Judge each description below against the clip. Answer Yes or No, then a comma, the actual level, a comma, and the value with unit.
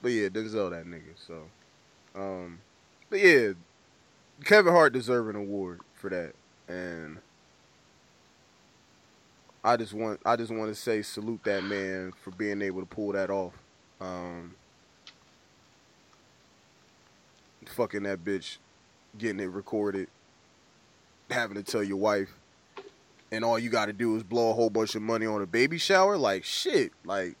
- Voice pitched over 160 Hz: No, low, 105 Hz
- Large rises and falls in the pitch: No, average, 3.4 semitones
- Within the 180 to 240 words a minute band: No, average, 145 wpm